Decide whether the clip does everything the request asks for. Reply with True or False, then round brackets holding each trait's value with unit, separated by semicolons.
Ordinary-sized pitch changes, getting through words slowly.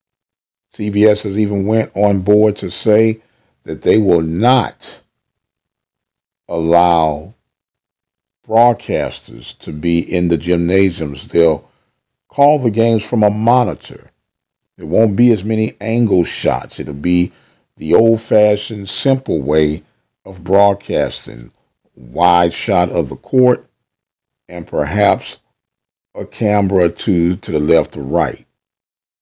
True (4.5 semitones; 120 wpm)